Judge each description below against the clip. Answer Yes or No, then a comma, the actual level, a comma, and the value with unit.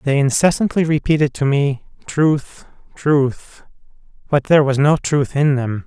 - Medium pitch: Yes, medium, 145 Hz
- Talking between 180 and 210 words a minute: No, average, 145 wpm